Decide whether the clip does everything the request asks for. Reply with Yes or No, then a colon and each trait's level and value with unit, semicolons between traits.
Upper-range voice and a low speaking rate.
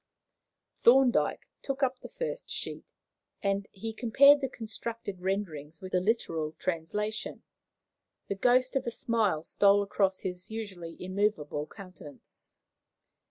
Yes: high, 205 Hz; slow, 125 wpm